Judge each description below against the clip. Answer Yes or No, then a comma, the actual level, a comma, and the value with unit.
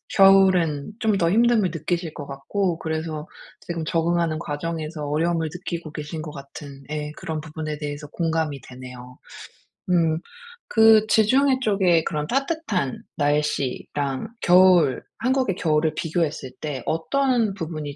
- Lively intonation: No, average, 4.0 semitones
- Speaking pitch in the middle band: Yes, medium, 165 Hz